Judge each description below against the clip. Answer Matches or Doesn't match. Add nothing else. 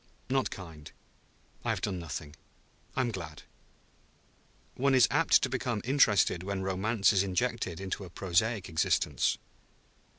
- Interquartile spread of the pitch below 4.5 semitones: Doesn't match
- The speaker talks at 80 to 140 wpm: Matches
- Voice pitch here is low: Matches